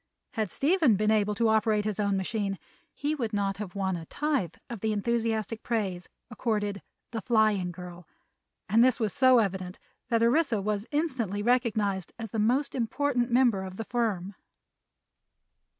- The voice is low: No, high, 220 Hz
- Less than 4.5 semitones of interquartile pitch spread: Yes, average, 3.2 semitones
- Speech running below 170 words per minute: Yes, average, 160 wpm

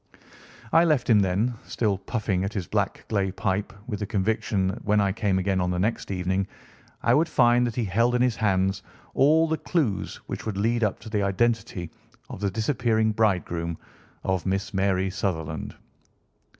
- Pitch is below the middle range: Yes, low, 100 Hz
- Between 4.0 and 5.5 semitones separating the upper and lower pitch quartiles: No, average, 3.5 semitones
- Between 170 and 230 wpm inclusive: Yes, average, 180 wpm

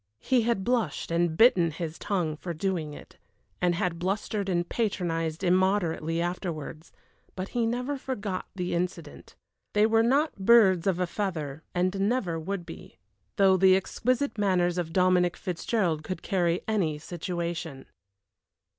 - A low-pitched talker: No, medium, 185 Hz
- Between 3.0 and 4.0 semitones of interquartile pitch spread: Yes, average, 3.3 semitones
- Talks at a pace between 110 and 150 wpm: Yes, average, 145 wpm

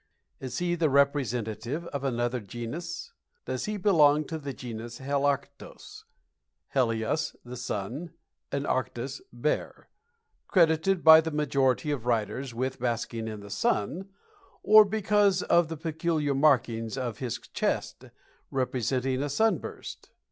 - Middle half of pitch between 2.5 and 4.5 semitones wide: No, average, 4.9 semitones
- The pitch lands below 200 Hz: Yes, medium, 140 Hz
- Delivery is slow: Yes, slow, 125 wpm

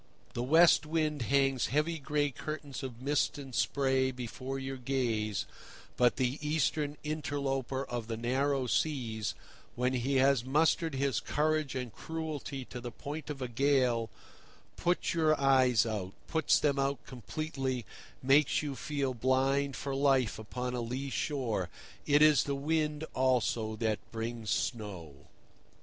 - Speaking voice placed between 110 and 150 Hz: Yes, low, 135 Hz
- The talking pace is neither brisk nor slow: Yes, average, 145 wpm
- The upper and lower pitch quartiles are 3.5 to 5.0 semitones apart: No, average, 3.1 semitones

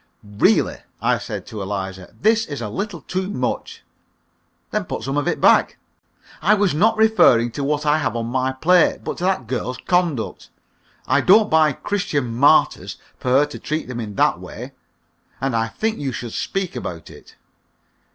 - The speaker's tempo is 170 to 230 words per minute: Yes, average, 180 wpm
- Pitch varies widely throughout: Yes, wide, 7.5 semitones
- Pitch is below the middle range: No, medium, 145 Hz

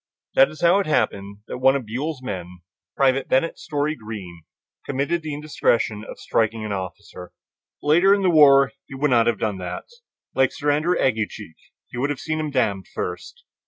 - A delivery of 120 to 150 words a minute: No, average, 185 wpm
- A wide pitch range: Yes, wide, 6.2 semitones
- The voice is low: Yes, low, 130 Hz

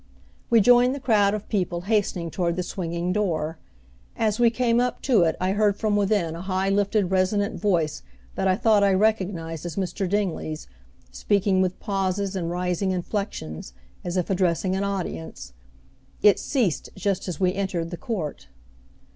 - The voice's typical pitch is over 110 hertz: Yes, high, 190 Hz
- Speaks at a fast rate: No, average, 165 wpm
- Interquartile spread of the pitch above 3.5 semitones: No, average, 2.9 semitones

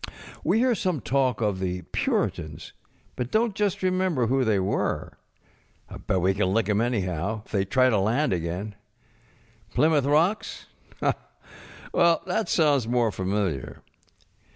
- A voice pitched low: Yes, low, 120 Hz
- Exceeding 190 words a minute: No, slow, 135 wpm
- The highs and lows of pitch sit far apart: Yes, wide, 8.4 semitones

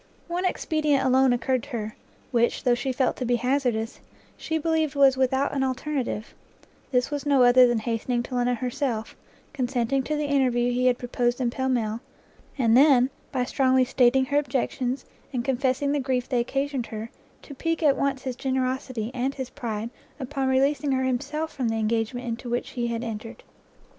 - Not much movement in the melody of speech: Yes, narrow, 2.2 semitones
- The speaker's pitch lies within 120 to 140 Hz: No, very high, 255 Hz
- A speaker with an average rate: Yes, average, 185 wpm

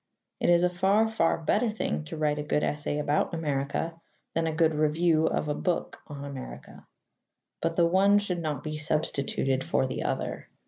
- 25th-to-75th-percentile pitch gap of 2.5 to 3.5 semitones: Yes, average, 2.8 semitones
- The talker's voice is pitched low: No, medium, 155 Hz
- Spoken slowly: No, average, 185 wpm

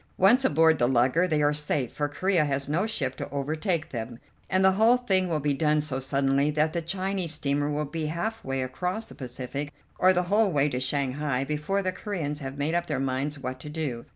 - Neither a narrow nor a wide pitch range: Yes, average, 4.6 semitones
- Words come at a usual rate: No, fast, 220 wpm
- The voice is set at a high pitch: No, medium, 150 Hz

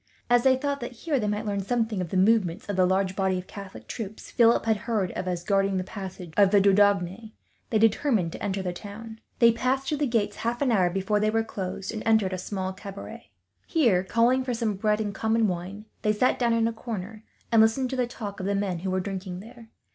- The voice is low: No, high, 210 Hz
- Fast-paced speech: Yes, fast, 240 wpm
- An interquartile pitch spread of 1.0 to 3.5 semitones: Yes, average, 3.2 semitones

